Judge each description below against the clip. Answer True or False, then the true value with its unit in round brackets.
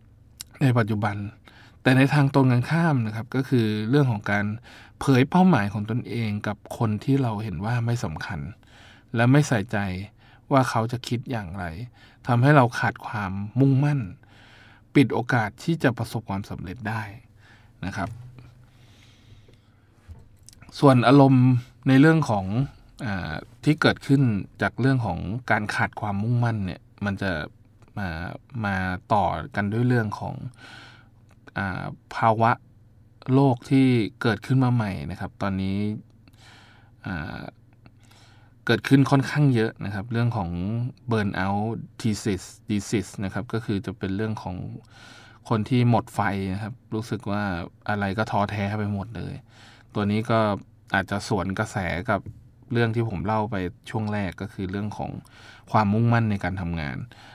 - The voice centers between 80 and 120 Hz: True (110 Hz)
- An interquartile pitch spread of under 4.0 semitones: True (3.0 semitones)